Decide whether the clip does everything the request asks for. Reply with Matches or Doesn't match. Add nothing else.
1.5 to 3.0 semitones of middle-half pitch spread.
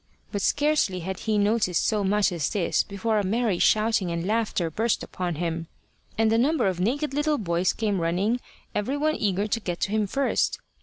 Doesn't match